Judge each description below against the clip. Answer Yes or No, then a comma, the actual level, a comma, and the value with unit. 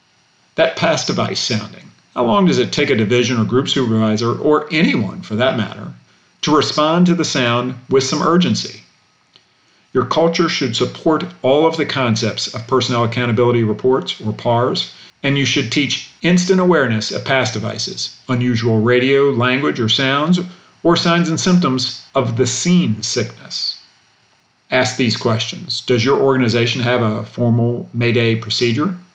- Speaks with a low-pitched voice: Yes, low, 130 Hz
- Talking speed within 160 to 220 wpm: No, average, 150 wpm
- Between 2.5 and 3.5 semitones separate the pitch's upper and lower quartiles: No, average, 4.3 semitones